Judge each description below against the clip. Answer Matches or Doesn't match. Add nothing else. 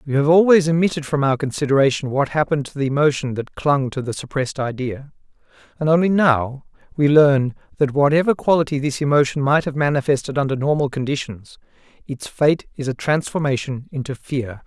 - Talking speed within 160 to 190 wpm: Matches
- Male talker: Matches